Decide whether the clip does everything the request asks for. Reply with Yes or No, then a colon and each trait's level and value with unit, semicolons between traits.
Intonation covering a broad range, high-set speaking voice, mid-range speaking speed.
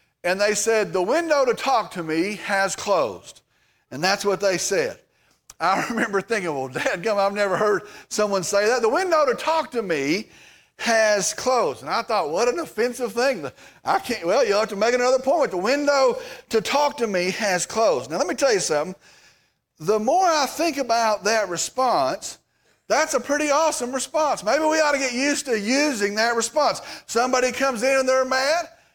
Yes: wide, 5.8 semitones; high, 240 Hz; average, 195 wpm